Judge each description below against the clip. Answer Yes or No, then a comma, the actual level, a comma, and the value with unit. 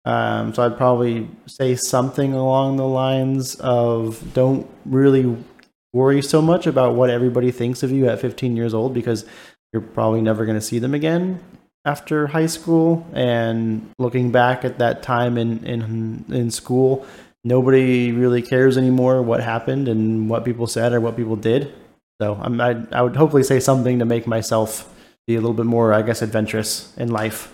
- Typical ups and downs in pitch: No, narrow, 2.3 semitones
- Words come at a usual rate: Yes, average, 180 wpm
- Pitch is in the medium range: No, low, 120 Hz